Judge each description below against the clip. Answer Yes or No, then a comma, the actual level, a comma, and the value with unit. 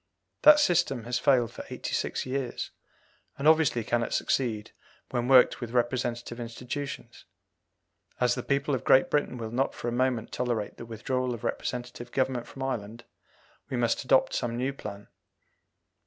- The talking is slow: No, average, 155 wpm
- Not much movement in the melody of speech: Yes, narrow, 2.1 semitones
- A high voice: No, low, 125 Hz